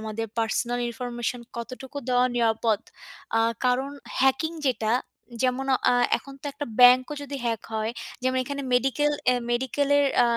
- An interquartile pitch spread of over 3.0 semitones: No, narrow, 2.4 semitones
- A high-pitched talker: Yes, very high, 250 Hz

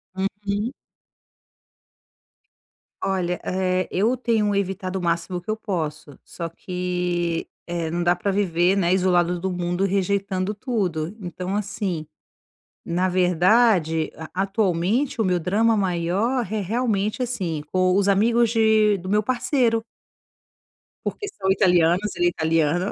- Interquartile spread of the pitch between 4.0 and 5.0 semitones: No, average, 3.2 semitones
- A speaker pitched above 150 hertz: Yes, medium, 185 Hz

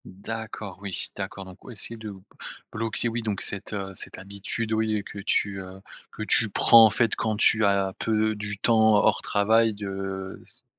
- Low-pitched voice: Yes, low, 105 Hz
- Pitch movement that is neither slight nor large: No, narrow, 2.3 semitones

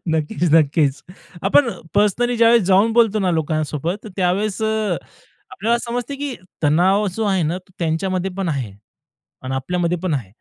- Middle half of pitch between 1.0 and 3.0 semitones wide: No, average, 5.3 semitones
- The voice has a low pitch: No, medium, 185 Hz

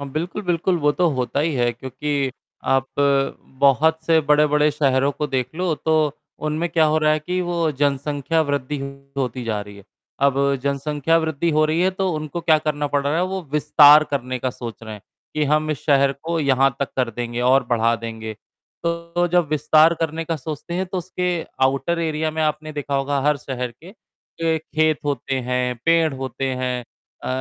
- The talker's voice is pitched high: No, medium, 150 Hz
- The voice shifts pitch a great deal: No, average, 3.2 semitones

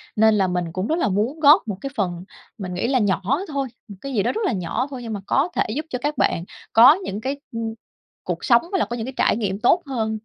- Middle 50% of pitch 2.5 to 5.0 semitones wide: No, wide, 5.4 semitones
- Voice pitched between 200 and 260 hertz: Yes, high, 230 Hz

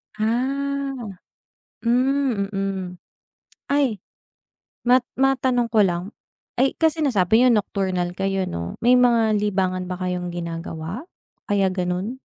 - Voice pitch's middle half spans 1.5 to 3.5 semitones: No, wide, 5.5 semitones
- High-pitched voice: Yes, high, 210 Hz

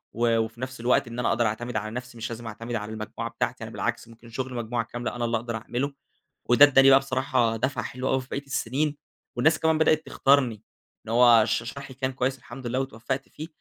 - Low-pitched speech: Yes, low, 120 Hz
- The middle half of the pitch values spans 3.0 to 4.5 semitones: No, narrow, 2.5 semitones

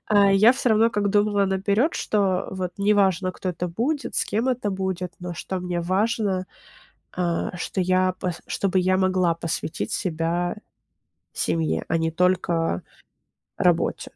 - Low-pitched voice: No, medium, 185 Hz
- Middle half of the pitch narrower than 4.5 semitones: Yes, narrow, 2.5 semitones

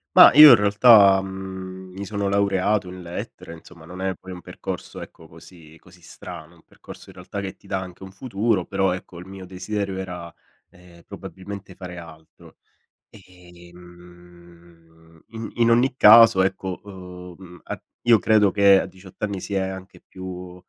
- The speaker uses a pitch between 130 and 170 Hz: No, very low, 95 Hz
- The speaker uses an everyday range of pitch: No, narrow, 2.1 semitones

